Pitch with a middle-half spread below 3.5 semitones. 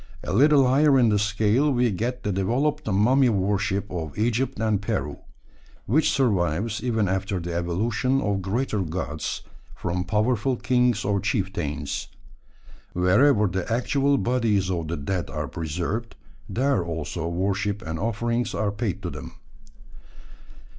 No: average, 5.0 semitones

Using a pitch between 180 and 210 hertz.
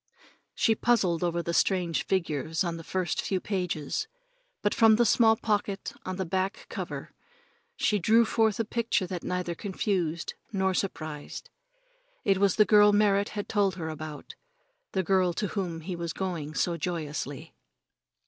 Yes: medium, 185 Hz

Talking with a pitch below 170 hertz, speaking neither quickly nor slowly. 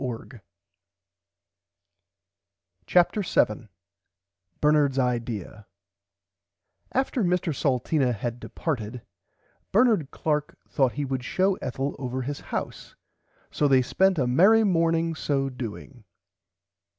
No: medium, 140 Hz; slow, 100 wpm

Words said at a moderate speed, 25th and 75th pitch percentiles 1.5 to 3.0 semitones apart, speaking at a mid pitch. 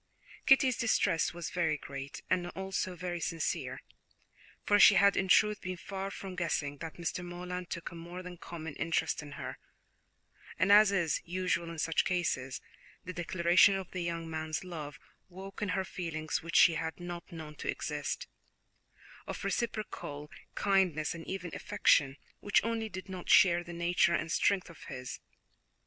Yes: average, 165 wpm; narrow, 2.6 semitones; medium, 175 Hz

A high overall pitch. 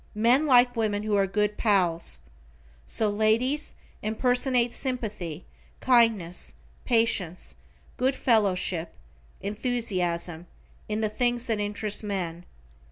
Yes: high, 215 Hz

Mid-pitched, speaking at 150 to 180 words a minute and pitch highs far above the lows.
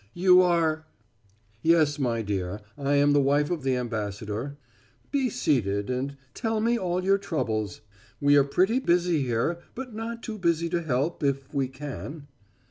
Yes: medium, 145 Hz; average, 165 wpm; wide, 5.9 semitones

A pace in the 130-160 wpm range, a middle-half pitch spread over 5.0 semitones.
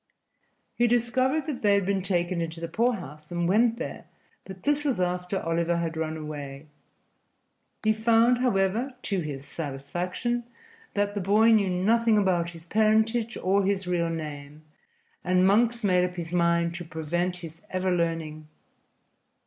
No: average, 155 wpm; average, 4.7 semitones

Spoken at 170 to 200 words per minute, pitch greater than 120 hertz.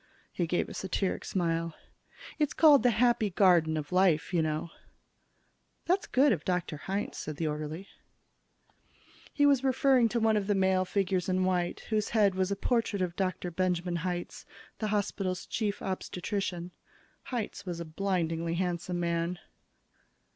No: average, 155 wpm; medium, 185 Hz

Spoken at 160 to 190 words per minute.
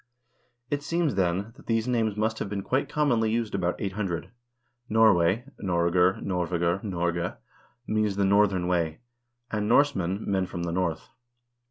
No: average, 145 wpm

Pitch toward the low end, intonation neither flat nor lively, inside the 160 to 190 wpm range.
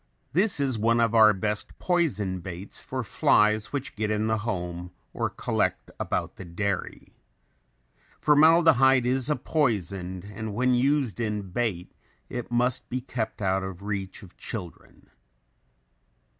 No: low, 110 Hz; average, 4.7 semitones; average, 140 wpm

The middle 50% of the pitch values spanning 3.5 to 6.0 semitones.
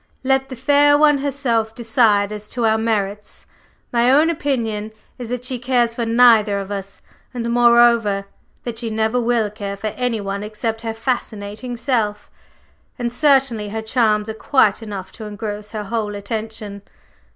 No: average, 2.7 semitones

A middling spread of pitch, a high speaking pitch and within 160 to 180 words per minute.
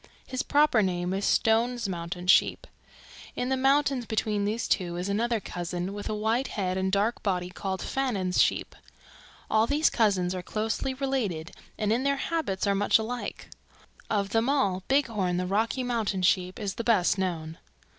Yes: average, 4.5 semitones; high, 210 Hz; average, 170 wpm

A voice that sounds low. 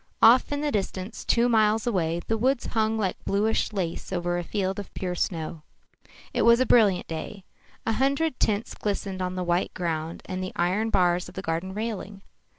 No: high, 195 Hz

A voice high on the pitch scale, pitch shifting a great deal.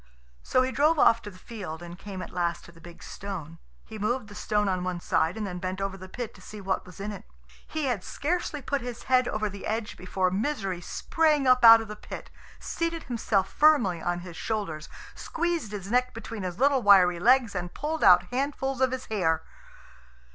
Yes: high, 210 Hz; wide, 5.7 semitones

